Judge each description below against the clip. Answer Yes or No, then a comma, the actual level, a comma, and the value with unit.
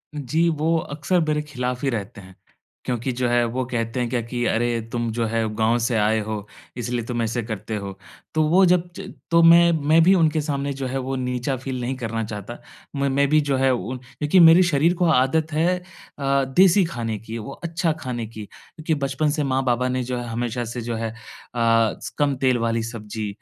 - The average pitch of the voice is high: No, low, 125 Hz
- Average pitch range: Yes, average, 4.5 semitones